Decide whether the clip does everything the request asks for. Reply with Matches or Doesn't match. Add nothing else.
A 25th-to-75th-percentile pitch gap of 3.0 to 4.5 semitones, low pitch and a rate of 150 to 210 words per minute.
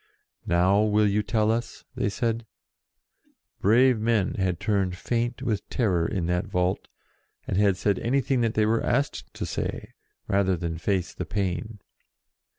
Matches